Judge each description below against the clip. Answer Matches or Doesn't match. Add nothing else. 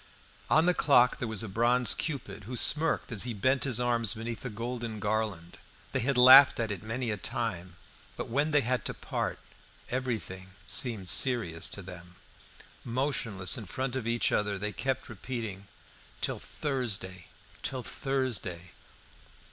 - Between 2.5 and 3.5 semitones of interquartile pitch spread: Doesn't match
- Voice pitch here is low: Matches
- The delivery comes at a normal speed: Matches